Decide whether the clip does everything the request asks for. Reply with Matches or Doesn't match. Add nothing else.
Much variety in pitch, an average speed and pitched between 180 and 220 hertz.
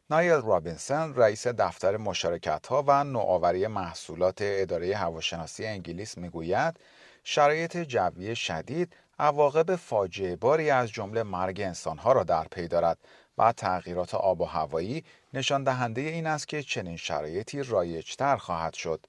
Doesn't match